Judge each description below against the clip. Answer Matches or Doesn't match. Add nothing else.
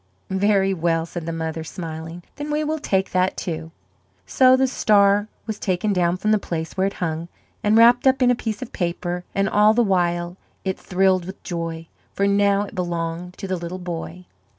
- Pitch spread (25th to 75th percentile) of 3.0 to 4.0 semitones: Matches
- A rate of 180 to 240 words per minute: Matches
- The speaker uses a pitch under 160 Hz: Doesn't match